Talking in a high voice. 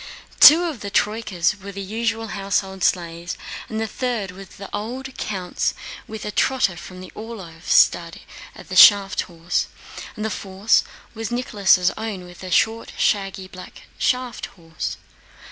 Yes: high, 200 Hz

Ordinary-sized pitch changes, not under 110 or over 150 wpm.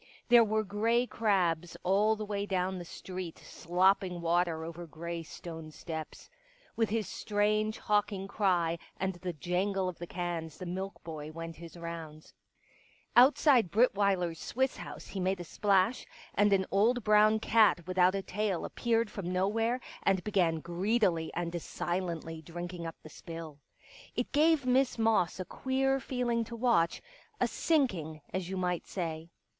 No: average, 4.1 semitones; average, 160 wpm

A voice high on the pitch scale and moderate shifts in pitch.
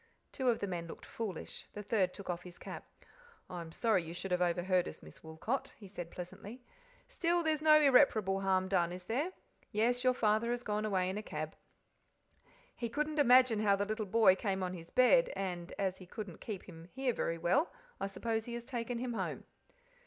Yes: high, 210 Hz; average, 4.9 semitones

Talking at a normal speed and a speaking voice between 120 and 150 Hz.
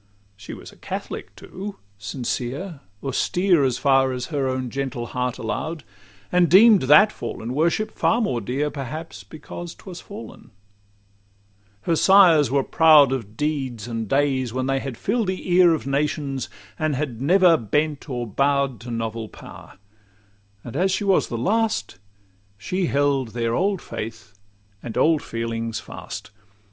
Yes: average, 150 wpm; medium, 140 Hz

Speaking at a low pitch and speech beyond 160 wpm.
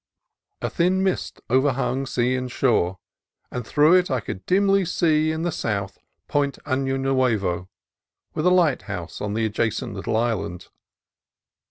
No: low, 130 Hz; average, 145 wpm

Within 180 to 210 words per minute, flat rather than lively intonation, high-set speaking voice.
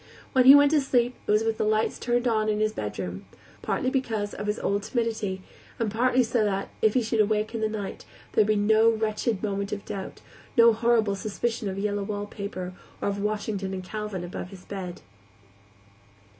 Yes: average, 200 wpm; narrow, 2.3 semitones; high, 215 Hz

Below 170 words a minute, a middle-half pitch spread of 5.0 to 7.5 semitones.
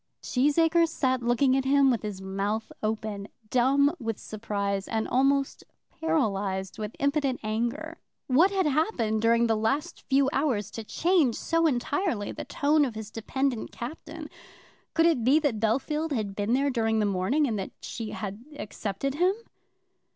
Yes: average, 160 wpm; average, 5.3 semitones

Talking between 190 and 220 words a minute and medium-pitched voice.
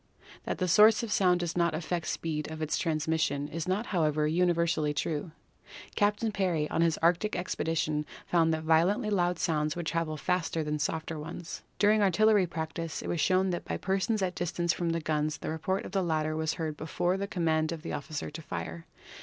Yes: fast, 205 wpm; medium, 165 Hz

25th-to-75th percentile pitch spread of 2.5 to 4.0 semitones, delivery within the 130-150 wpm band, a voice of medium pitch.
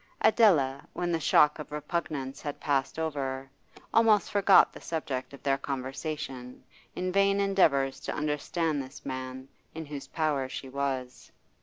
Yes: average, 3.4 semitones; average, 145 wpm; medium, 145 Hz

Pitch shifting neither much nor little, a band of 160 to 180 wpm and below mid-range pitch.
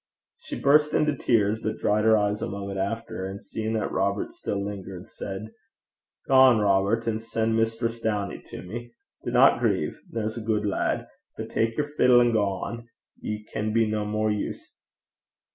No: narrow, 2.1 semitones; average, 170 wpm; low, 110 Hz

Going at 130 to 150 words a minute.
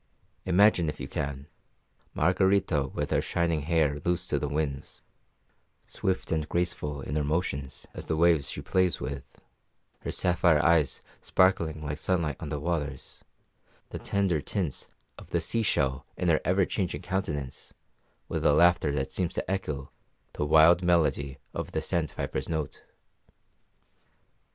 Yes: average, 145 wpm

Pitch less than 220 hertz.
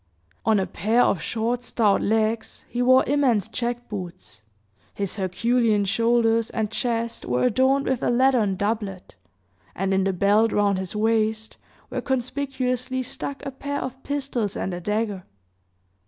No: high, 225 Hz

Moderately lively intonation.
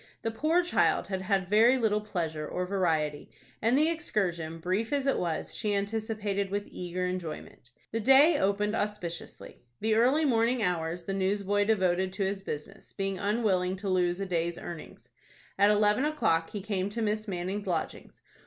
Yes: average, 3.4 semitones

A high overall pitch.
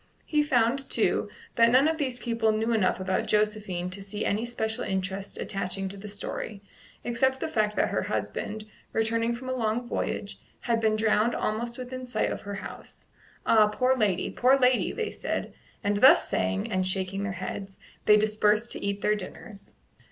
Yes: high, 215 Hz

